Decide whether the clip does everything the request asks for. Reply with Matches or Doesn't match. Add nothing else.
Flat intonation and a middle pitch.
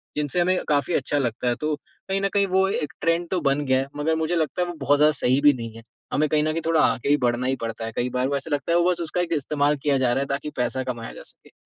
Doesn't match